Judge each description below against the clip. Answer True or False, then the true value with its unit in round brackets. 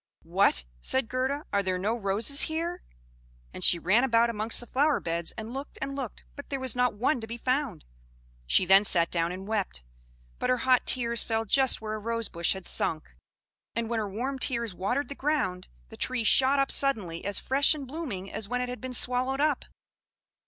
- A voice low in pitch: False (235 Hz)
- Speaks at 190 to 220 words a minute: True (200 wpm)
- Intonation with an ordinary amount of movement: True (4.9 semitones)